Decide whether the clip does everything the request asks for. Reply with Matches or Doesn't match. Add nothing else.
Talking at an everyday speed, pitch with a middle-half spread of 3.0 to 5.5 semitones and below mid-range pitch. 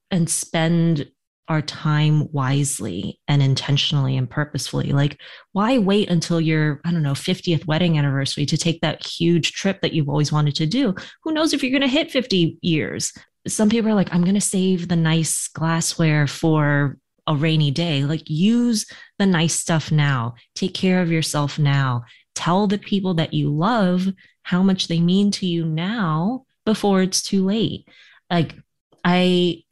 Doesn't match